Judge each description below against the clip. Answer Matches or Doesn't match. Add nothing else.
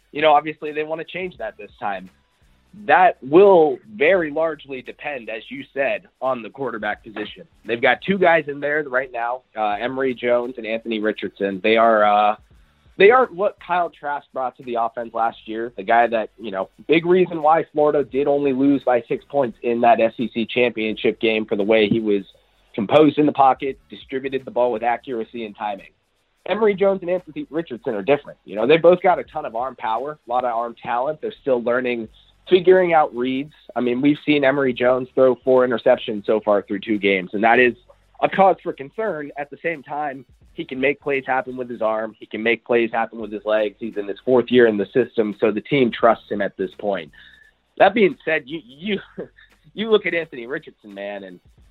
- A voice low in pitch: Matches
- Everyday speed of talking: Doesn't match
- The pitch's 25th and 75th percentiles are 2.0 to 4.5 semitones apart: Doesn't match